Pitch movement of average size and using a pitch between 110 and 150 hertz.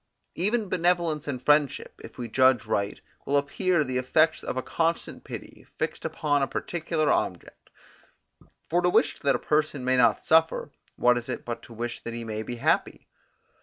Yes: average, 4.8 semitones; medium, 140 Hz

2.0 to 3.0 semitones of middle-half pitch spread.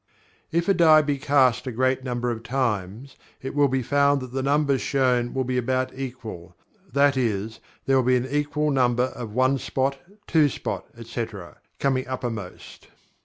Yes: narrow, 2.4 semitones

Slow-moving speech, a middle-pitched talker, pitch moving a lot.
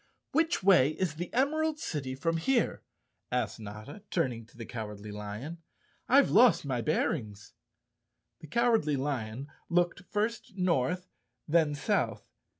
Yes: slow, 130 wpm; medium, 155 Hz; wide, 8.4 semitones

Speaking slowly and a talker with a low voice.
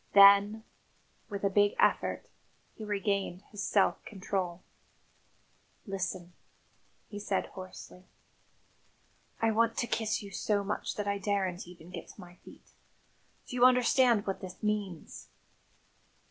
No: slow, 130 wpm; high, 200 Hz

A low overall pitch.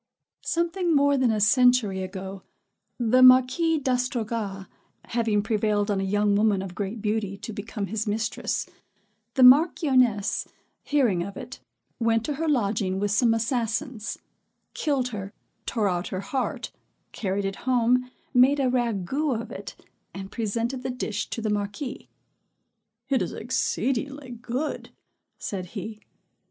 No: high, 225 Hz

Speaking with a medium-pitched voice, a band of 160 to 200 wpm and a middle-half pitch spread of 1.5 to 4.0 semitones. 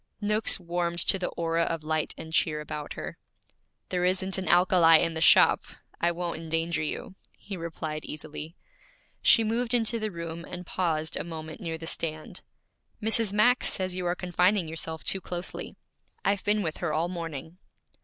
Yes: medium, 170 Hz; average, 175 wpm; narrow, 2.6 semitones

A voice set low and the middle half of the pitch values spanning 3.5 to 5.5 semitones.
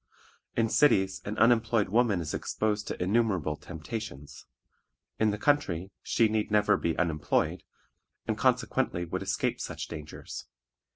Yes: low, 100 Hz; average, 4.3 semitones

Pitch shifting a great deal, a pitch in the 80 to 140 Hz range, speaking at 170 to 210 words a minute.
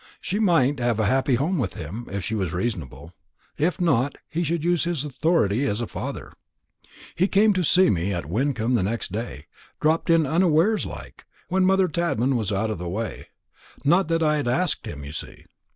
Yes: wide, 8.1 semitones; low, 135 Hz; average, 195 wpm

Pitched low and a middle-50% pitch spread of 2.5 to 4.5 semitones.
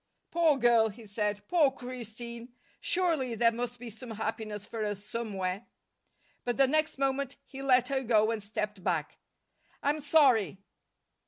No: high, 235 Hz; average, 4.1 semitones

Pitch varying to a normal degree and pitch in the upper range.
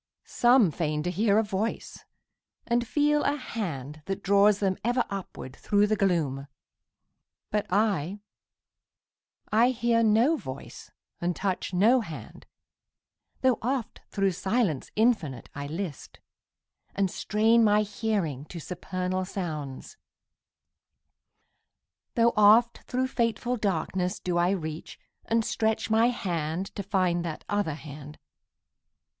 Yes: average, 4.9 semitones; high, 200 Hz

